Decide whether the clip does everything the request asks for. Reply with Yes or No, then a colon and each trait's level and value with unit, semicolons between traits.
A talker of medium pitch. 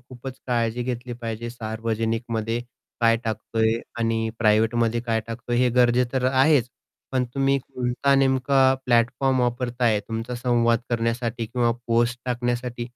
No: low, 120 Hz